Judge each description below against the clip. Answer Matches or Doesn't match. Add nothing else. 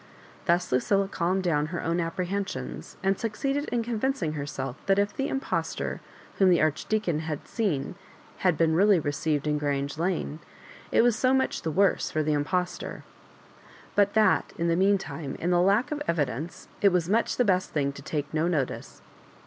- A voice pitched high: Doesn't match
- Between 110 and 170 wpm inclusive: Doesn't match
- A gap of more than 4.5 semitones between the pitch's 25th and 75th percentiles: Matches